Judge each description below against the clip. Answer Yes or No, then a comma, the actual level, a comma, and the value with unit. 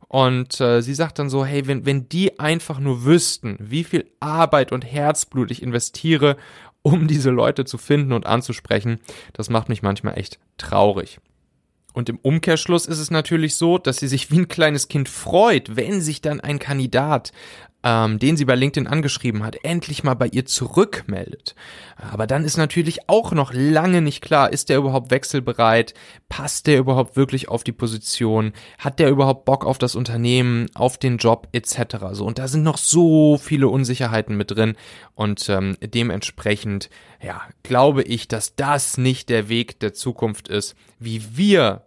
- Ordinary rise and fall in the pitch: Yes, average, 4.2 semitones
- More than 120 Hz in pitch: Yes, low, 130 Hz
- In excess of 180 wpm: No, average, 175 wpm